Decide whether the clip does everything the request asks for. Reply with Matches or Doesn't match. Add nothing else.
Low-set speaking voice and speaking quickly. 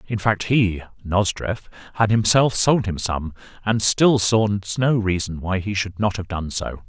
Doesn't match